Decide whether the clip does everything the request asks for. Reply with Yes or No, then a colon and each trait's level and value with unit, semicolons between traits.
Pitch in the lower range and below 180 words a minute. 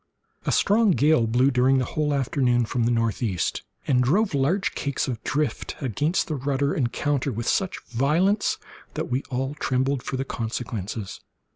Yes: low, 130 Hz; average, 170 wpm